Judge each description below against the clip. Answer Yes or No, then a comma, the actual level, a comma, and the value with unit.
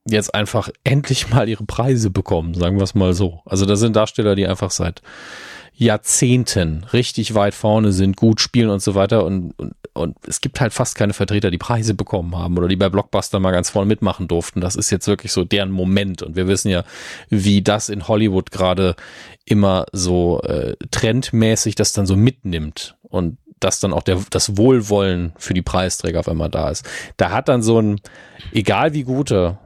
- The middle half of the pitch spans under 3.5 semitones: Yes, average, 3.1 semitones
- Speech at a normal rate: No, fast, 195 wpm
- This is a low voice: Yes, low, 100 Hz